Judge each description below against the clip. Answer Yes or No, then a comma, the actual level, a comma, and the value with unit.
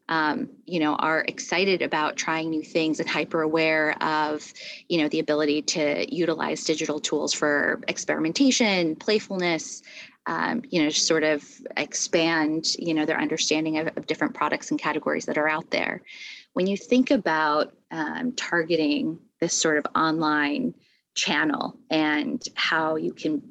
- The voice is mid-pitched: Yes, medium, 160 Hz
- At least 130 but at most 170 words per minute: Yes, average, 150 wpm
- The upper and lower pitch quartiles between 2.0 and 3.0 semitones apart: Yes, average, 2.7 semitones